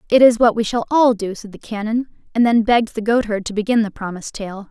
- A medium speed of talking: No, fast, 255 wpm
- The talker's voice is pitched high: Yes, high, 220 Hz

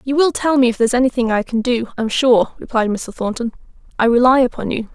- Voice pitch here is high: Yes, high, 240 Hz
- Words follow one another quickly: Yes, fast, 245 wpm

